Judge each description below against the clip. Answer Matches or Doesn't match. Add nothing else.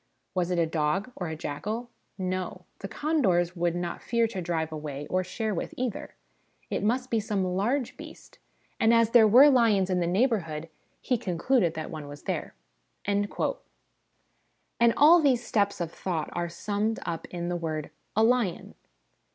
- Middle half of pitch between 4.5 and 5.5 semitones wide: Matches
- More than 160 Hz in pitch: Matches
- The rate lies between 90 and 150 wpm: Doesn't match